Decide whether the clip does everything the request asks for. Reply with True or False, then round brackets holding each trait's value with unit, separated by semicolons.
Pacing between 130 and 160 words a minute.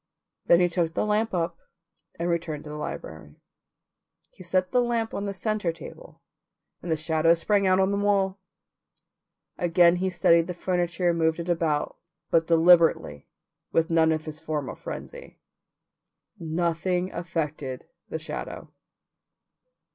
True (145 wpm)